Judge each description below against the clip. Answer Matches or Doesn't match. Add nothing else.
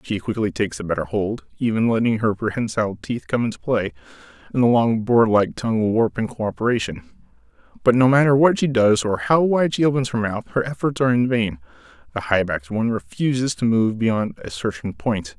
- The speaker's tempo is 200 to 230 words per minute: Matches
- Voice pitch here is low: Matches